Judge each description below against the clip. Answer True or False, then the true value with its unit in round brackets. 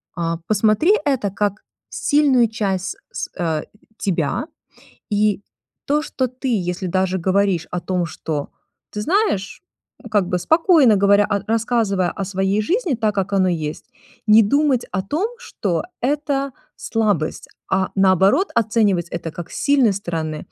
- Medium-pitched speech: False (200 Hz)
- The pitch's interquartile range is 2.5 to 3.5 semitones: False (5.1 semitones)